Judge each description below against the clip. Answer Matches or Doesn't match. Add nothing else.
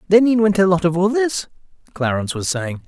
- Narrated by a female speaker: Doesn't match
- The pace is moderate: Doesn't match